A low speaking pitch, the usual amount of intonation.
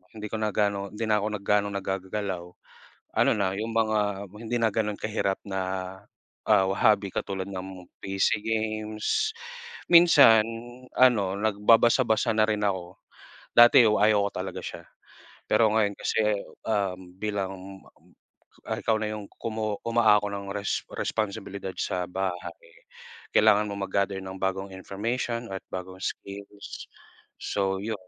No: low, 100 Hz; narrow, 2.1 semitones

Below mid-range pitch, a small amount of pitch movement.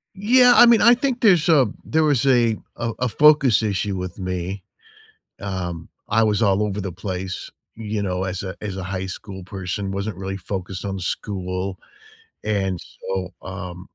No: low, 100 Hz; average, 3.6 semitones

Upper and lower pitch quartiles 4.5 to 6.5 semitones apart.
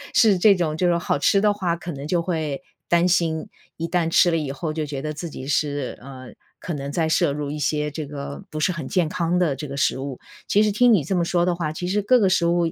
No: average, 3.5 semitones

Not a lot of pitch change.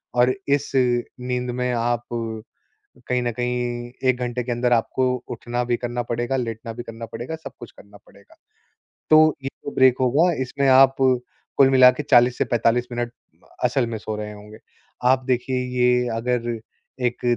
Yes: narrow, 1.2 semitones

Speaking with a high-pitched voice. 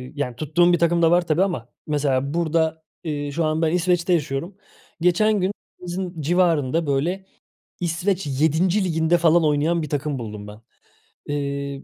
No: medium, 160 Hz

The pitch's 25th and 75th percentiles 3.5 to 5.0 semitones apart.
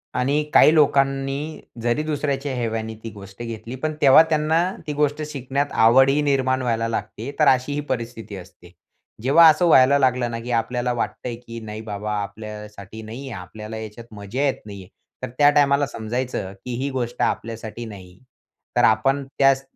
Yes: average, 4.1 semitones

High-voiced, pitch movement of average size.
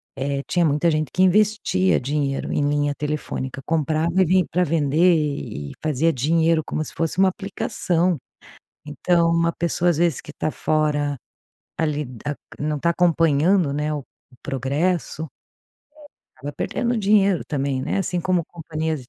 No: medium, 160 Hz; average, 3.2 semitones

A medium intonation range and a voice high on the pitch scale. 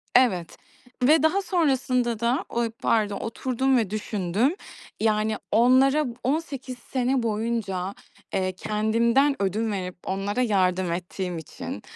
Yes: average, 4.8 semitones; high, 225 Hz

